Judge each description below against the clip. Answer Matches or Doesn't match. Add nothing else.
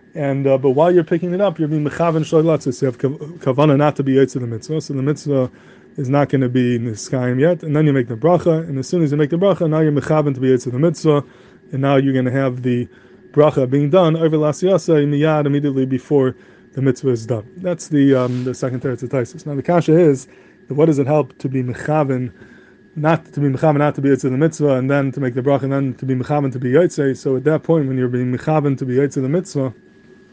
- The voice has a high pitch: Doesn't match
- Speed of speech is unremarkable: Doesn't match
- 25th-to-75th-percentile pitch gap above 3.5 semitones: Doesn't match